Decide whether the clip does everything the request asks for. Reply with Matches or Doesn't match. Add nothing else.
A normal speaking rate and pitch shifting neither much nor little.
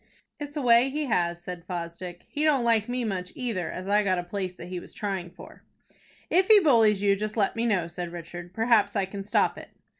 Doesn't match